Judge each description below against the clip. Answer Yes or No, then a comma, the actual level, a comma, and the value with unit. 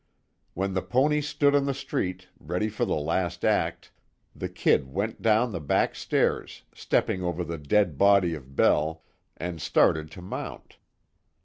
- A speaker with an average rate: Yes, average, 155 wpm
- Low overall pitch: Yes, very low, 90 Hz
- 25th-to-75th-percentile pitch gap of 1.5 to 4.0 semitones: No, average, 5.0 semitones